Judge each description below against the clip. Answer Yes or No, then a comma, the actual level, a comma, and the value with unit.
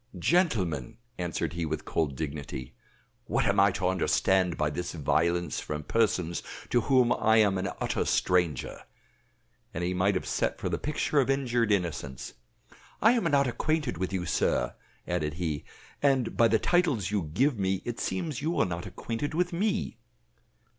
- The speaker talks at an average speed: Yes, average, 165 wpm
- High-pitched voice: No, very low, 95 Hz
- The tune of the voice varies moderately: No, wide, 7.8 semitones